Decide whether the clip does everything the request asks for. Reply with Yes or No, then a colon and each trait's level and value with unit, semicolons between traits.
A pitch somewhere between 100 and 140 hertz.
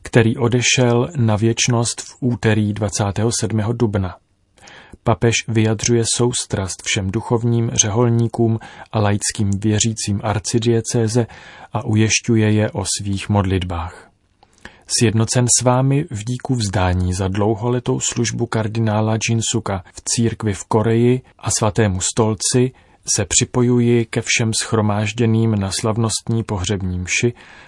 Yes: low, 115 Hz